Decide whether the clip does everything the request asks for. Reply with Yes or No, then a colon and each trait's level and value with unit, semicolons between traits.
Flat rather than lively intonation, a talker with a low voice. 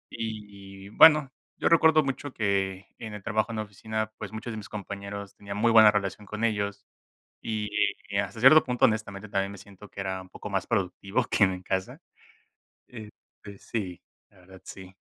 Yes: narrow, 2.0 semitones; low, 105 Hz